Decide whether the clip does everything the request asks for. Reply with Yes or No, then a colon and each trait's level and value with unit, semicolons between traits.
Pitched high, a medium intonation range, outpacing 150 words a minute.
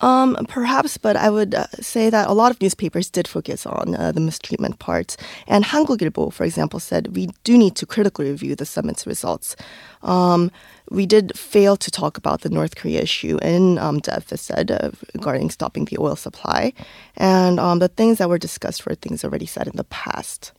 Yes: high, 200 Hz; average, 4.2 semitones; average, 190 wpm